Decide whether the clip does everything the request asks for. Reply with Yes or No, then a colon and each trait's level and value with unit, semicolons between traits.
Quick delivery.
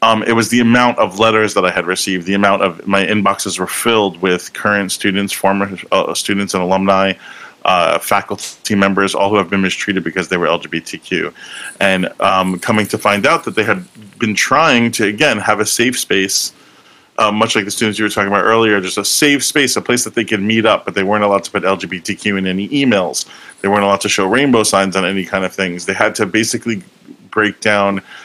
Yes: fast, 220 wpm